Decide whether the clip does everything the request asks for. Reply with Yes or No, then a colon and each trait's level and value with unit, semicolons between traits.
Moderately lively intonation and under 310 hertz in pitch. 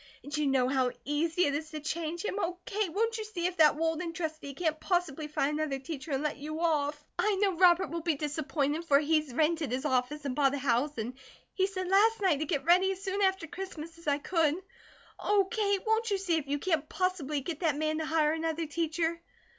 No: average, 3.6 semitones; very high, 320 Hz